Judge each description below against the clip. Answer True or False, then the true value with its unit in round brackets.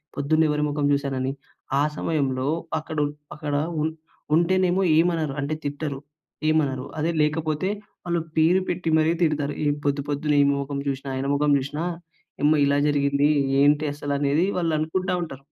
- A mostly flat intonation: True (2.1 semitones)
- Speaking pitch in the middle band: True (150 Hz)